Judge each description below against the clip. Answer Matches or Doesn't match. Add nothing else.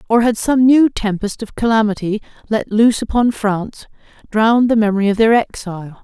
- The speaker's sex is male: Doesn't match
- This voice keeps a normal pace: Matches